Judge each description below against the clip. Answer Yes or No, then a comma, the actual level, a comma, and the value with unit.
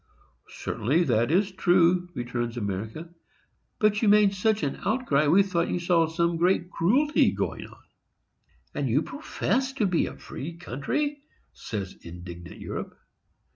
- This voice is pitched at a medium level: Yes, medium, 170 Hz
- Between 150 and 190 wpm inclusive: No, average, 140 wpm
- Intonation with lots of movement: Yes, wide, 8.1 semitones